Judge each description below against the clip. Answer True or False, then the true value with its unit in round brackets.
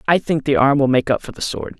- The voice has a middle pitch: True (145 Hz)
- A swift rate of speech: True (335 wpm)